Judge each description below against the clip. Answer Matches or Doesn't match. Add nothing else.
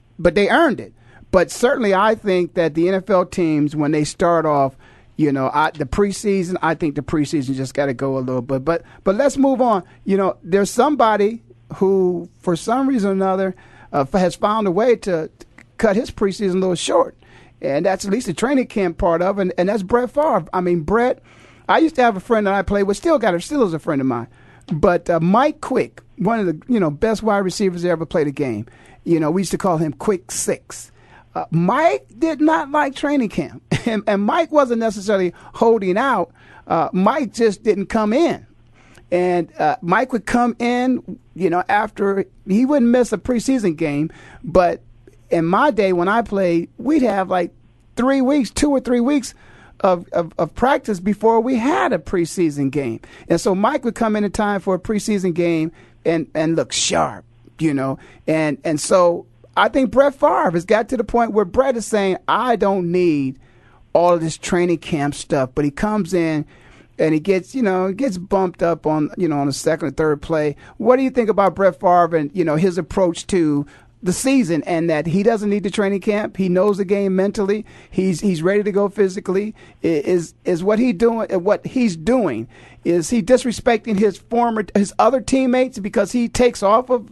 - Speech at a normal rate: Doesn't match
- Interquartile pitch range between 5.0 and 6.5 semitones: Matches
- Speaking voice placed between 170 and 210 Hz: Matches